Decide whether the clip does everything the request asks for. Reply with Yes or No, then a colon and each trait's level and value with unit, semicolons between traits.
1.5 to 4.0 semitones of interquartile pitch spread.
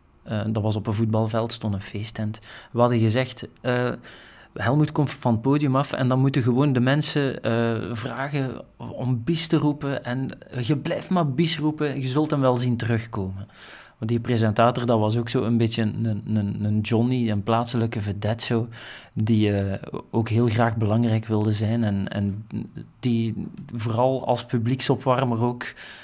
Yes: average, 2.9 semitones